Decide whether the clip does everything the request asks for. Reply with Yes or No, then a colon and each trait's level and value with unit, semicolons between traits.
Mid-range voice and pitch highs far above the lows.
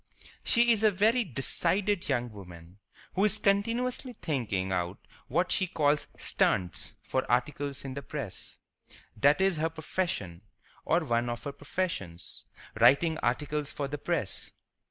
Yes: medium, 145 Hz; wide, 7.8 semitones